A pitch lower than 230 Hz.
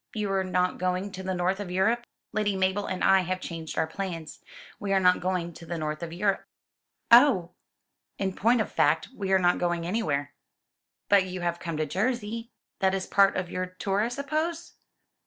Yes: high, 190 Hz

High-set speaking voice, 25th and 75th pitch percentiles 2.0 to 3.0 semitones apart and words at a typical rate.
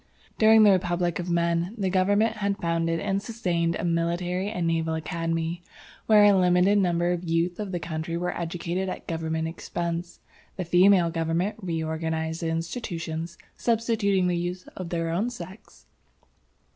No: medium, 175 Hz; narrow, 2.5 semitones; average, 160 wpm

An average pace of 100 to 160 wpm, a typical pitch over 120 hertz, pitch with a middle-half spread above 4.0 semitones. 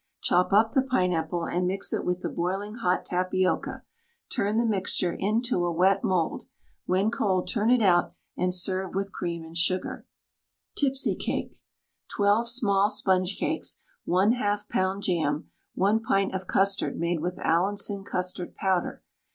No: average, 150 wpm; high, 190 Hz; narrow, 2.4 semitones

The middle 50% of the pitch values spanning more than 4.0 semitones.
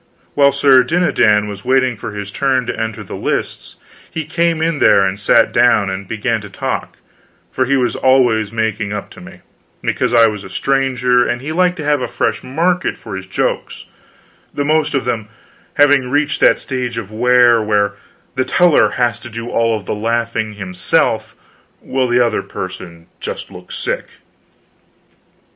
Yes: average, 4.5 semitones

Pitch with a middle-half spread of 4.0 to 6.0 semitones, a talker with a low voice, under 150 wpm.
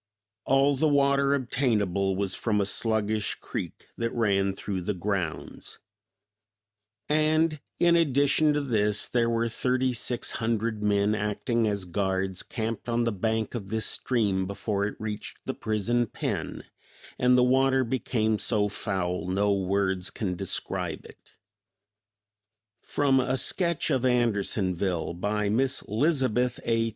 Yes: average, 4.3 semitones; low, 110 Hz; slow, 135 wpm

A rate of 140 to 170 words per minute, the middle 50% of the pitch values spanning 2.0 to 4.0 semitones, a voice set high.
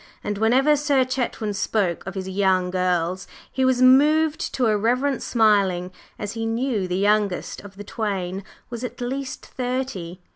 No: average, 155 wpm; average, 5.1 semitones; high, 215 Hz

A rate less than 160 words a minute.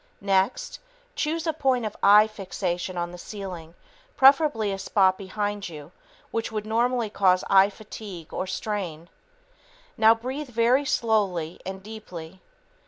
Yes: slow, 135 wpm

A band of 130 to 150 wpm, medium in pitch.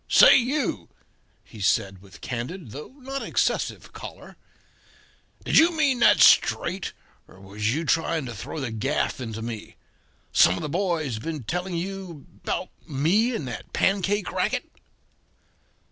Yes: average, 145 wpm; medium, 155 Hz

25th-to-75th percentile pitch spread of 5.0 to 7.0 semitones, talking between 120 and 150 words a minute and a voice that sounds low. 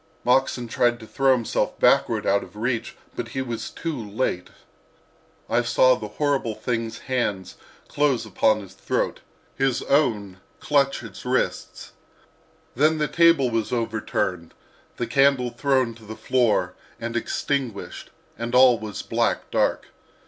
No: average, 3.3 semitones; average, 140 wpm; low, 120 Hz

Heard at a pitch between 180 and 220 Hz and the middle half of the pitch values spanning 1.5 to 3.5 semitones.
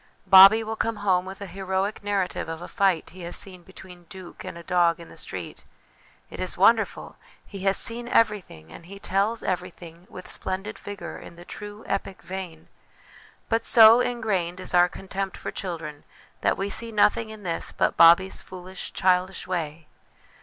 Yes: high, 190 Hz; narrow, 2.6 semitones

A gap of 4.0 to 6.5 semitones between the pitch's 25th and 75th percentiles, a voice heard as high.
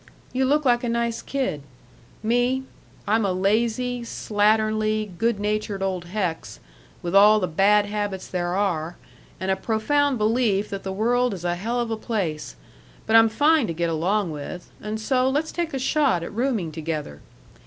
Yes: average, 4.3 semitones; high, 215 Hz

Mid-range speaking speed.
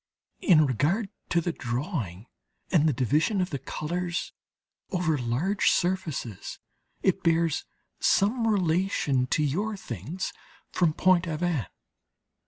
No: slow, 115 wpm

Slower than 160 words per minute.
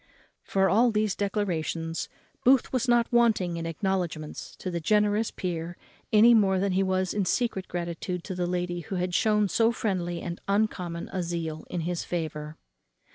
No: average, 170 wpm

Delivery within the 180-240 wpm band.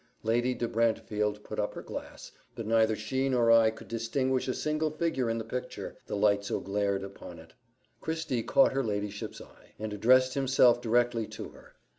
Yes: average, 185 wpm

